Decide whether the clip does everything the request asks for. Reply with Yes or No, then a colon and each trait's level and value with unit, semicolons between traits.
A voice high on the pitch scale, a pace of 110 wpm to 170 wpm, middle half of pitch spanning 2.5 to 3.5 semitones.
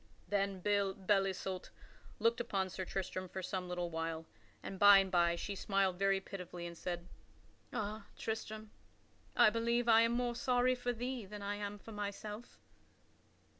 Yes: high, 200 Hz; average, 160 wpm; average, 3.0 semitones